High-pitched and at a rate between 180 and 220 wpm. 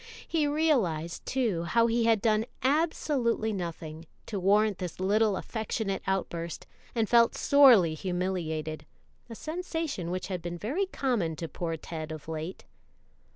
No: high, 195 Hz; average, 140 wpm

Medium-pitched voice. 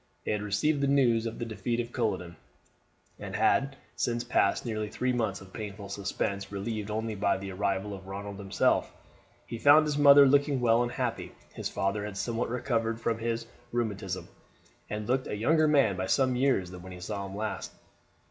No: low, 110 Hz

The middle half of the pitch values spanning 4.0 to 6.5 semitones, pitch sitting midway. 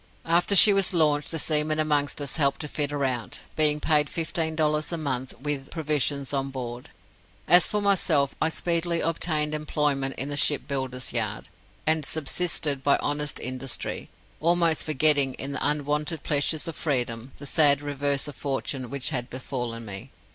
No: narrow, 2.6 semitones; medium, 145 Hz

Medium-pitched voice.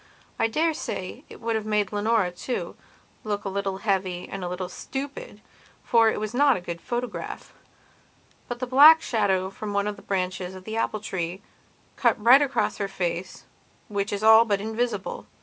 No: high, 210 Hz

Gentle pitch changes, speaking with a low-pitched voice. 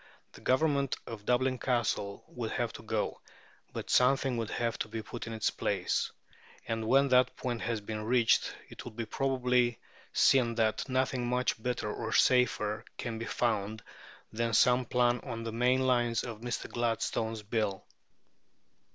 Yes: narrow, 2.1 semitones; low, 120 Hz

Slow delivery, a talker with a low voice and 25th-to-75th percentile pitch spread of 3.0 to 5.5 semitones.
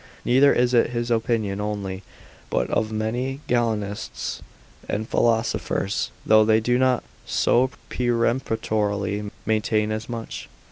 No: slow, 120 wpm; low, 110 Hz; narrow, 2.4 semitones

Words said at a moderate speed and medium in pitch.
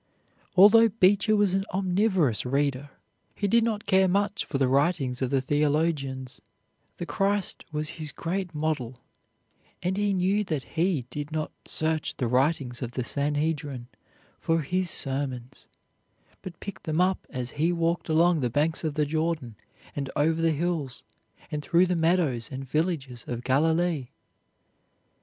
Yes: average, 150 wpm; medium, 155 Hz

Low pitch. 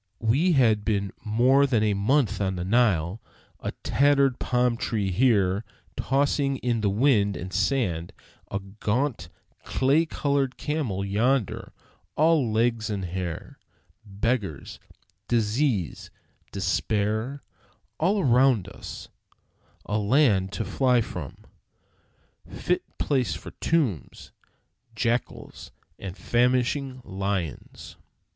Yes: low, 115 Hz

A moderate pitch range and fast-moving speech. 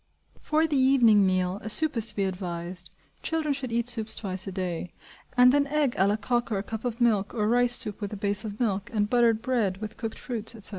Yes: average, 3.8 semitones; fast, 240 wpm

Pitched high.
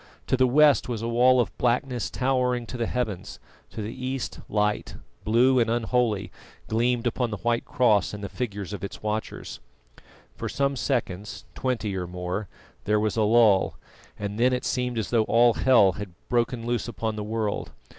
No: low, 115 Hz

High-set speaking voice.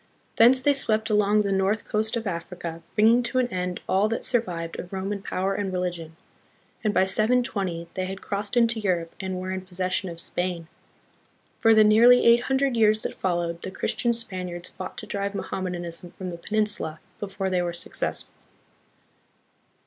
Yes: high, 195 Hz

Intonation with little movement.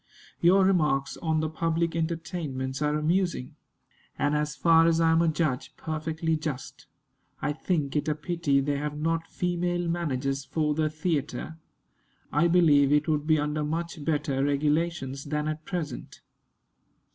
Yes: narrow, 2.2 semitones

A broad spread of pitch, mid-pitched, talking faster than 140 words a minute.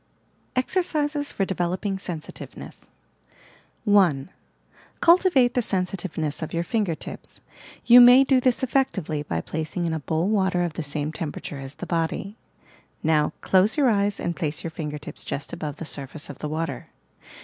Yes: wide, 6.3 semitones; medium, 175 Hz; average, 160 wpm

